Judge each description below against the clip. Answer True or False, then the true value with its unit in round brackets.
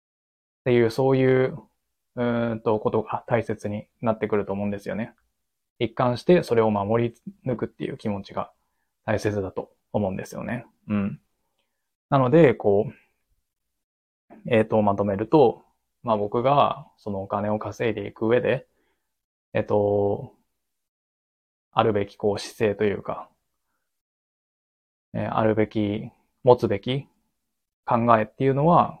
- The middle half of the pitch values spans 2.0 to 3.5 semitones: True (2.9 semitones)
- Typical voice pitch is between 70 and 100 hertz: False (110 Hz)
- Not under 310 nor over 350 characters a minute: False (255 characters per minute)